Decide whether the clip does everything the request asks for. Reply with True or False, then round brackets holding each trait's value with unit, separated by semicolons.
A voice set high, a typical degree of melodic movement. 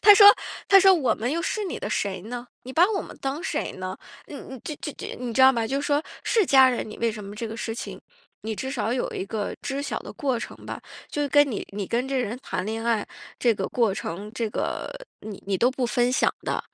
True (245 Hz; 4.4 semitones)